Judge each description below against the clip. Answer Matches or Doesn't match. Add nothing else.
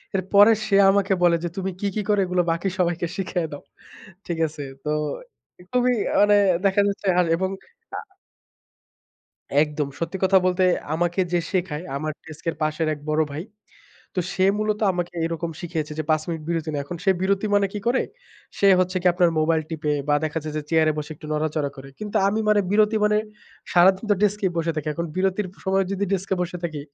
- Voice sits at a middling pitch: Matches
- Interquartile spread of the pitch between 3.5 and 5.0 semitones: Matches